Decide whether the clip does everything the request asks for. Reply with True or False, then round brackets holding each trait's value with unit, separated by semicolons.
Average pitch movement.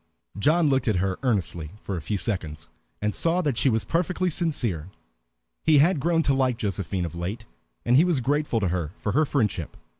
False (8.4 semitones)